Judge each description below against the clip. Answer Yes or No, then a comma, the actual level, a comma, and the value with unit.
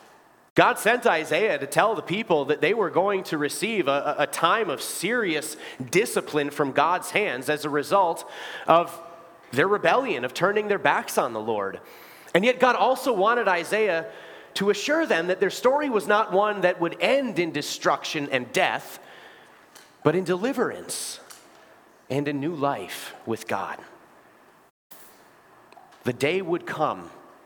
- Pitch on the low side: No, medium, 175 Hz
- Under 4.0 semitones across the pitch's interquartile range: No, wide, 5.5 semitones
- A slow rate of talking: No, average, 155 wpm